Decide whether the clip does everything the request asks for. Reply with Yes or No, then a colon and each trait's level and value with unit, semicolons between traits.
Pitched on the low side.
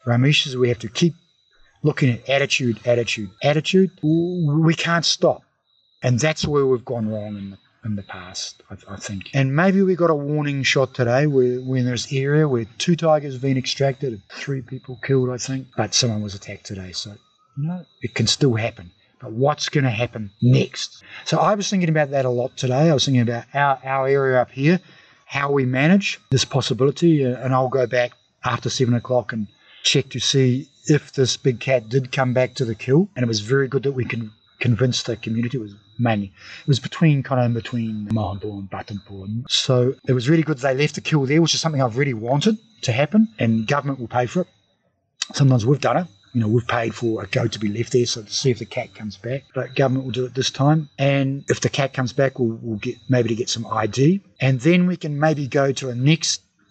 Yes: low, 130 Hz